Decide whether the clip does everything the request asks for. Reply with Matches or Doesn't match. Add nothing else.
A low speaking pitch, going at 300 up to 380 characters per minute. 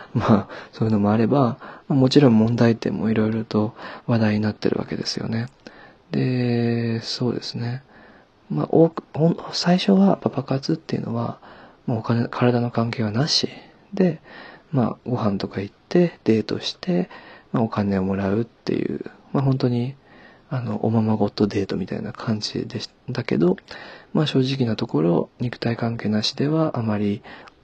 Matches